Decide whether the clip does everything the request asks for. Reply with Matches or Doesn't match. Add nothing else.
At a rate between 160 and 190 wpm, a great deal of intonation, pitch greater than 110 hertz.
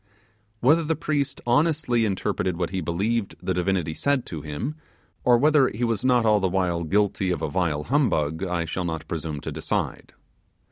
Doesn't match